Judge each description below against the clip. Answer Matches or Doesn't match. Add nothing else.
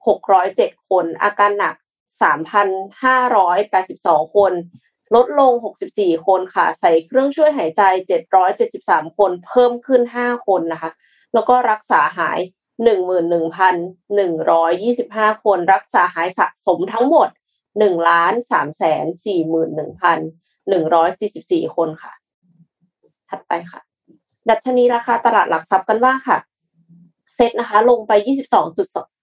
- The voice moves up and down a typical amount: Doesn't match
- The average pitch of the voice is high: Matches